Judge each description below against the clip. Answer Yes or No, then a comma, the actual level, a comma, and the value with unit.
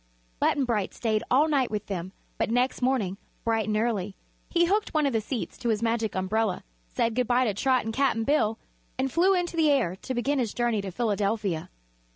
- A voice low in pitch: No, high, 230 Hz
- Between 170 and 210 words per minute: Yes, fast, 205 wpm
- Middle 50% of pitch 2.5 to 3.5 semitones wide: No, average, 4.0 semitones